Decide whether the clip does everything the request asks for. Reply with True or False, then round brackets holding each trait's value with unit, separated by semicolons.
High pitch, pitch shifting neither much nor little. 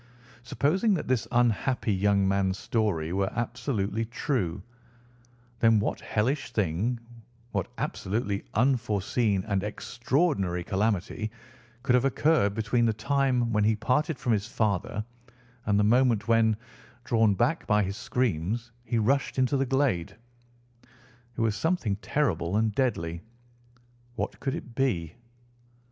False (110 Hz; 4.0 semitones)